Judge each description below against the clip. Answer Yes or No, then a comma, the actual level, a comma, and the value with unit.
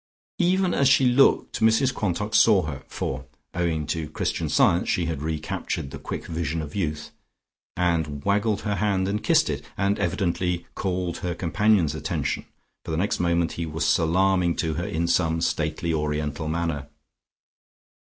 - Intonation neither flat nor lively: Yes, average, 4.0 semitones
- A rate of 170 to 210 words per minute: No, average, 160 wpm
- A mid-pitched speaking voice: No, very low, 85 Hz